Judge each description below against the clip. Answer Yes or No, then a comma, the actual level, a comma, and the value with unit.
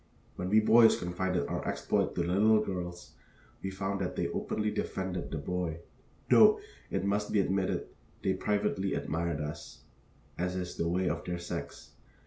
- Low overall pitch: Yes, very low, 90 Hz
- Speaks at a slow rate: No, average, 165 wpm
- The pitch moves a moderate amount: No, narrow, 2.2 semitones